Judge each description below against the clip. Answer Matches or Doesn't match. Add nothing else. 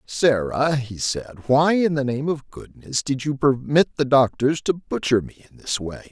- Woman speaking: Doesn't match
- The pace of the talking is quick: Doesn't match